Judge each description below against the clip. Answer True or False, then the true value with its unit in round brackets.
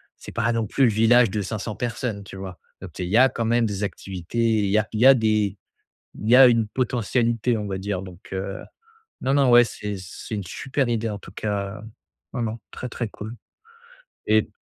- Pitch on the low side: True (110 Hz)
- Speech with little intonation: False (3.0 semitones)